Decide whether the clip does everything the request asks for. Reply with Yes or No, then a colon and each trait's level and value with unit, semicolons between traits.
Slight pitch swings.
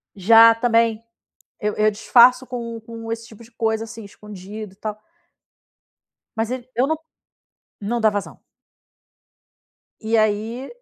Yes: narrow, 1.6 semitones